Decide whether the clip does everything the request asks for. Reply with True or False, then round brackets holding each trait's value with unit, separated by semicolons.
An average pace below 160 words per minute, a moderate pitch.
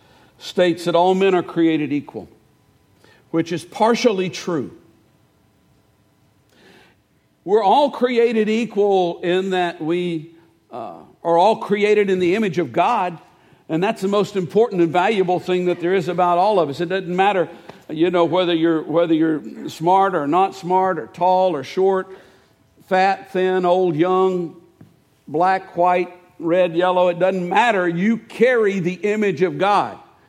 True (150 wpm; 180 Hz)